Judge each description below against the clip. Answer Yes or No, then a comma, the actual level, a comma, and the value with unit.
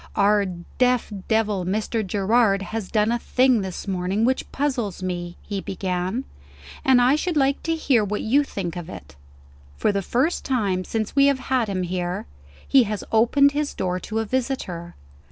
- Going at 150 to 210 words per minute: Yes, average, 175 wpm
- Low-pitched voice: No, high, 215 Hz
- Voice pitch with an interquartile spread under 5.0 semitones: No, wide, 5.4 semitones